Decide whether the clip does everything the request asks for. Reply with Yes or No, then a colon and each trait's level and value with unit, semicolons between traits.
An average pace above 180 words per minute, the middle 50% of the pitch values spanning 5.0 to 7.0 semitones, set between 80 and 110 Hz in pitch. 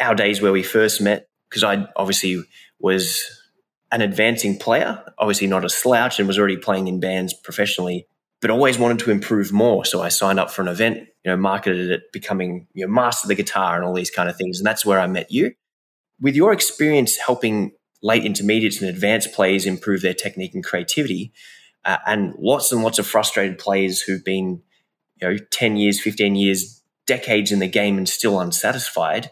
No: average, 200 wpm; narrow, 2.5 semitones; low, 100 Hz